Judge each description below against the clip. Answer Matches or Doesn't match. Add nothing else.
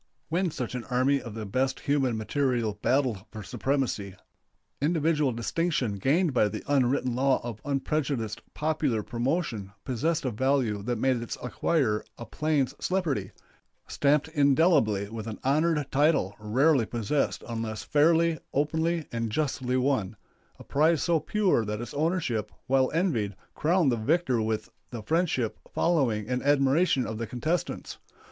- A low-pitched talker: Matches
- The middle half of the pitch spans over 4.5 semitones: Matches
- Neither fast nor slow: Matches